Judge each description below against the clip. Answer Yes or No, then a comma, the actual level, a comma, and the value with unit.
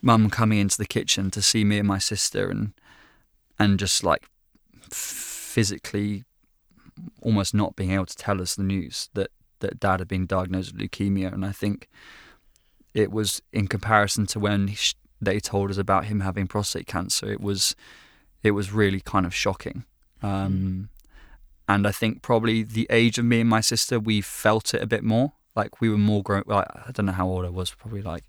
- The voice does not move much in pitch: Yes, narrow, 2.1 semitones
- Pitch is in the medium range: No, low, 100 Hz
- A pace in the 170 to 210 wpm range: Yes, average, 195 wpm